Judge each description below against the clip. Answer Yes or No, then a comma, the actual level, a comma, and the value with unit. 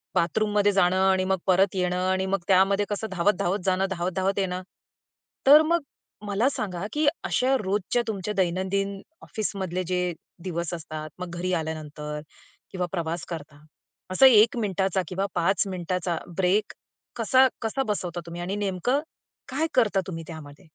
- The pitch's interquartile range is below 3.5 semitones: Yes, average, 2.8 semitones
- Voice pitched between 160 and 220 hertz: Yes, high, 190 Hz